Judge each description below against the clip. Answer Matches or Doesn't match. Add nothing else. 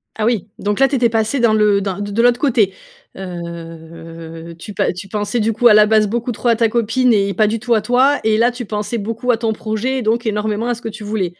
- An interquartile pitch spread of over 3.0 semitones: Doesn't match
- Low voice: Doesn't match